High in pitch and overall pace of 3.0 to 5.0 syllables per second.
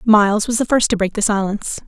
No: high, 210 Hz; 6.3 syllables/s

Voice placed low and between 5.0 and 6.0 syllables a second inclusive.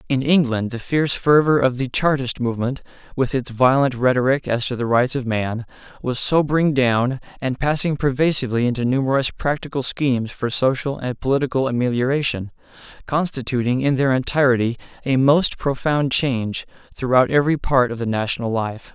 Yes: low, 130 Hz; 5.5 syllables/s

